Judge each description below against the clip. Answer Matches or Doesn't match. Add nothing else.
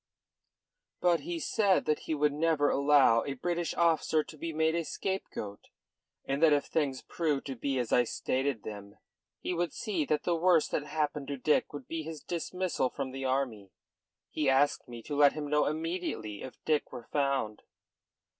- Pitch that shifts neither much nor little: Matches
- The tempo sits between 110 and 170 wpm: Doesn't match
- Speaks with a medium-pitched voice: Matches